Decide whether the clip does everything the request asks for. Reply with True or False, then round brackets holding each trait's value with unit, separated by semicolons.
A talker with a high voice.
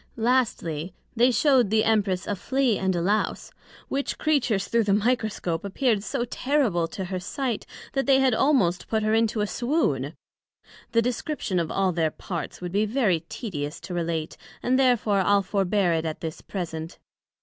True (205 Hz)